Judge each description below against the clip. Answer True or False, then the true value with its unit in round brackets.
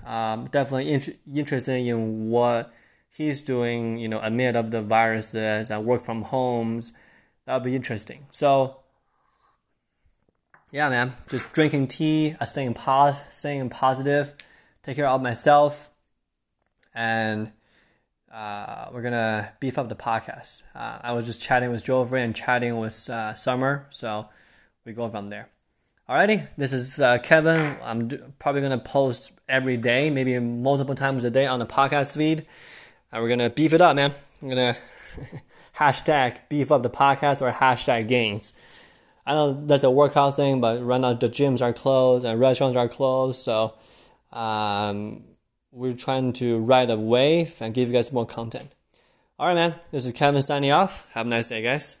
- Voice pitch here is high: False (125 Hz)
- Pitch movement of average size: True (3.4 semitones)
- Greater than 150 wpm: True (170 wpm)